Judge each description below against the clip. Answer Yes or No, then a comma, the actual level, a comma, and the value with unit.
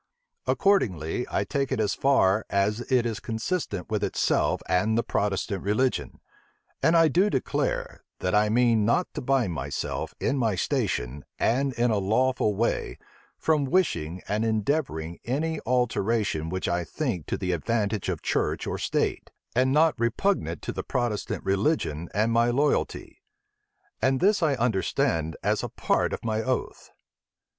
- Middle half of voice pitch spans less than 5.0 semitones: No, wide, 5.4 semitones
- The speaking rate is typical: Yes, average, 155 wpm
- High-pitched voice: No, low, 115 Hz